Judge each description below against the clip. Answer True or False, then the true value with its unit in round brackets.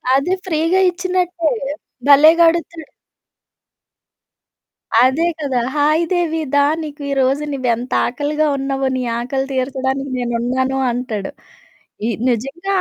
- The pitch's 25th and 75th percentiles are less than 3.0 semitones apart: False (3.9 semitones)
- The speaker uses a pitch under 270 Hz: False (275 Hz)